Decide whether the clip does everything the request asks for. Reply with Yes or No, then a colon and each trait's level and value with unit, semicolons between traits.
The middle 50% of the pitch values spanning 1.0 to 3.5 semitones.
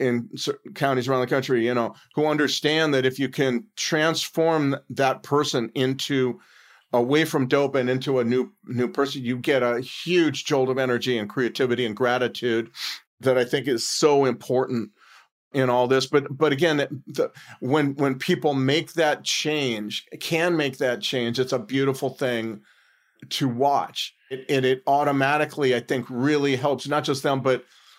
Yes: average, 2.7 semitones